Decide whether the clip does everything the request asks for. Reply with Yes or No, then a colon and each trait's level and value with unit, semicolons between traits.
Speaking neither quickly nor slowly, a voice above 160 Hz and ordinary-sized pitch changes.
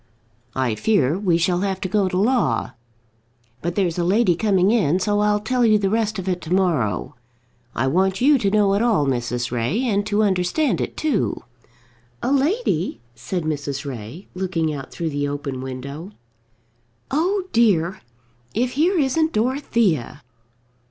No: average, 160 wpm; high, 190 Hz; wide, 6.5 semitones